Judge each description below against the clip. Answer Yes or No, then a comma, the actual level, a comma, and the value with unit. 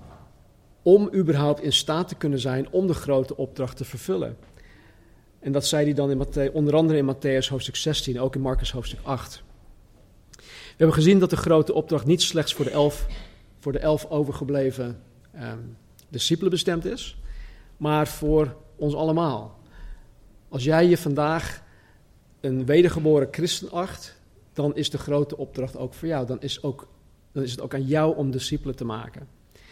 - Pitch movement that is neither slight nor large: Yes, average, 4.0 semitones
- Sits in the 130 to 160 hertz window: Yes, medium, 140 Hz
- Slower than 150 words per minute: No, average, 170 wpm